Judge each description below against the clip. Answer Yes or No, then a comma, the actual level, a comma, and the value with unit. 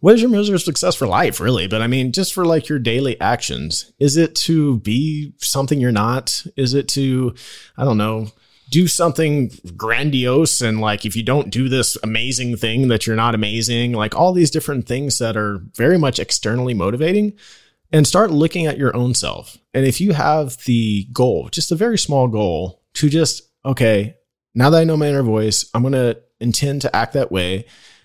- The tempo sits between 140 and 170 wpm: No, average, 200 wpm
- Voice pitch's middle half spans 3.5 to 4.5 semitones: No, average, 5.2 semitones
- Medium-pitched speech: No, low, 130 Hz